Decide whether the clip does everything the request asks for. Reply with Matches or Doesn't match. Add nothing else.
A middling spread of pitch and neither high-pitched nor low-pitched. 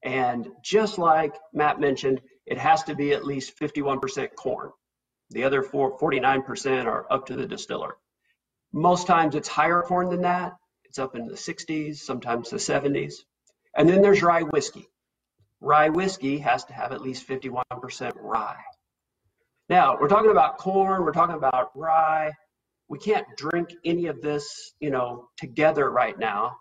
Matches